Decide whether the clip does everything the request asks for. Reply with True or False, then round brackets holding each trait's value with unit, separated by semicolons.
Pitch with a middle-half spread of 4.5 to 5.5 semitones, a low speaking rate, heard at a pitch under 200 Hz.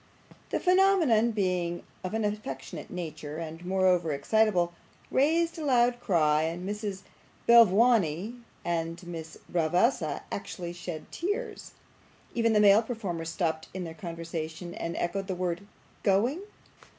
True (5.2 semitones; 125 wpm; 185 Hz)